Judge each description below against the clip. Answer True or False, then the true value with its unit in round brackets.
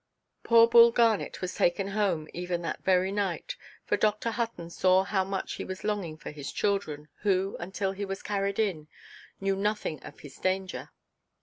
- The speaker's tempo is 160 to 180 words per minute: True (175 wpm)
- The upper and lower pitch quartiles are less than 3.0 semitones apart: True (2.5 semitones)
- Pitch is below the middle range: False (195 Hz)